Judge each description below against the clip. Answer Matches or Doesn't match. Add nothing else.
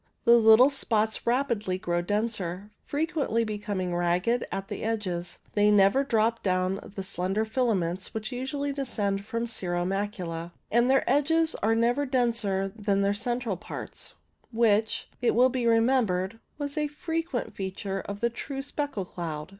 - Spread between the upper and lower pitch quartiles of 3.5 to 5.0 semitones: Matches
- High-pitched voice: Matches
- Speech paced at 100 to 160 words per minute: Matches